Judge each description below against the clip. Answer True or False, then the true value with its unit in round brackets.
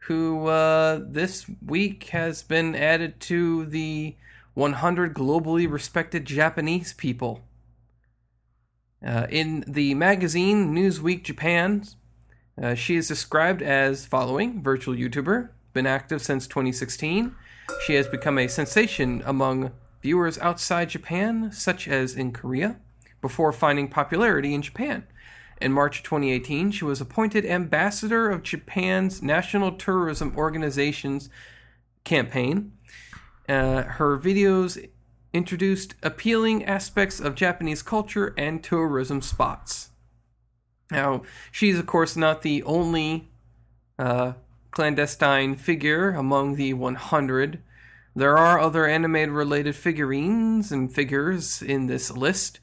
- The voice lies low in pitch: False (150 Hz)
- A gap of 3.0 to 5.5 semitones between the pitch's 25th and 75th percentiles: True (4.8 semitones)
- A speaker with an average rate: False (110 wpm)